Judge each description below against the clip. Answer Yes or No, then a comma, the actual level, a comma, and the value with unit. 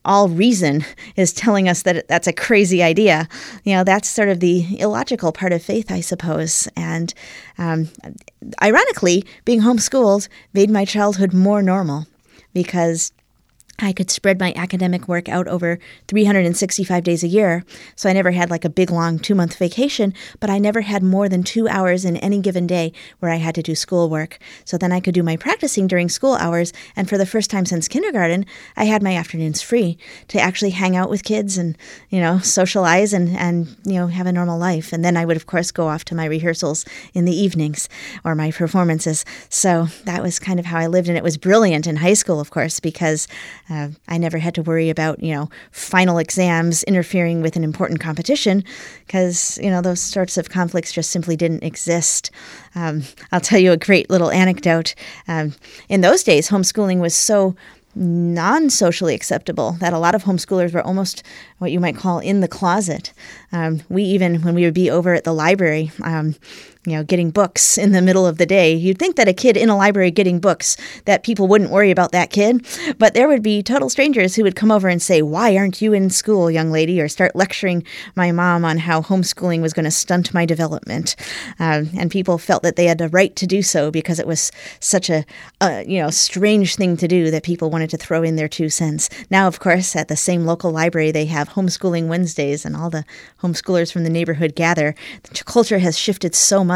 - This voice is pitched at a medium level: Yes, medium, 180 Hz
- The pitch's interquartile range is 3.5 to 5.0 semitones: No, average, 2.9 semitones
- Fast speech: Yes, fast, 215 wpm